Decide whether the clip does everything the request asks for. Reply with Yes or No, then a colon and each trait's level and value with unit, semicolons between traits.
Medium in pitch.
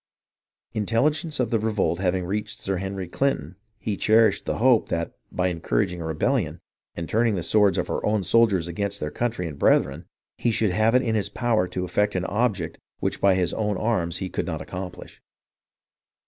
No: low, 100 Hz